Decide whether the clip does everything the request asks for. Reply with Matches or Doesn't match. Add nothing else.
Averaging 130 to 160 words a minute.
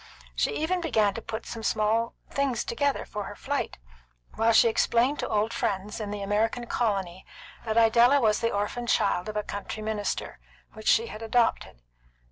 Doesn't match